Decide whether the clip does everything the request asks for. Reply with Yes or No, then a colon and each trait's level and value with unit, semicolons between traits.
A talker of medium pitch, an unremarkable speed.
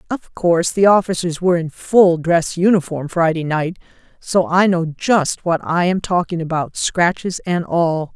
Yes: medium, 175 Hz; average, 170 wpm